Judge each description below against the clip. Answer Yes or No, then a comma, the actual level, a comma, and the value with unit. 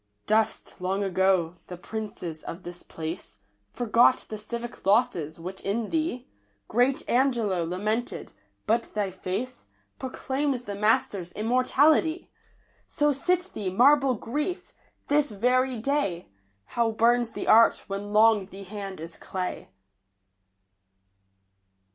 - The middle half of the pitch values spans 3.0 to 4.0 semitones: No, average, 4.9 semitones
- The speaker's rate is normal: No, slow, 120 wpm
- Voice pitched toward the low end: No, high, 220 Hz